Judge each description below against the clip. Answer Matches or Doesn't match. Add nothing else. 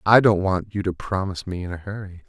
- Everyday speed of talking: Doesn't match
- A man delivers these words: Matches